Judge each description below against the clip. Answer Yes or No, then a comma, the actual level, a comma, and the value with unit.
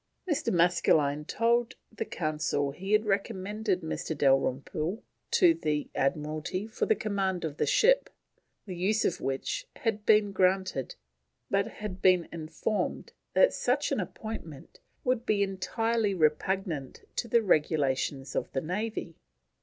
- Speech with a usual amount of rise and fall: No, wide, 5.7 semitones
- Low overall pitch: No, medium, 185 Hz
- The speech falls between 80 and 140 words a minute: Yes, slow, 135 wpm